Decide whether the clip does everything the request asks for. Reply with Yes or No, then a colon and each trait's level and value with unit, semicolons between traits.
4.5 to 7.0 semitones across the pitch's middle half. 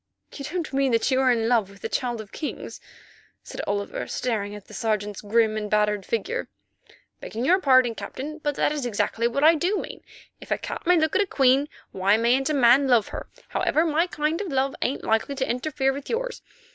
Yes: average, 5.2 semitones